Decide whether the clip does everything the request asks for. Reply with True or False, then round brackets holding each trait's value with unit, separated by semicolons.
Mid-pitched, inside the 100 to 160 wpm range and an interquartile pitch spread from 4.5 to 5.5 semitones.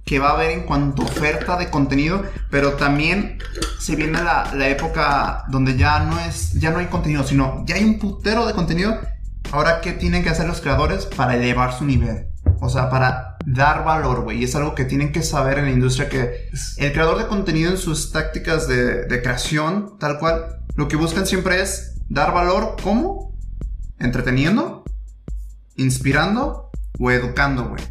False (145 Hz; 185 wpm; 4.8 semitones)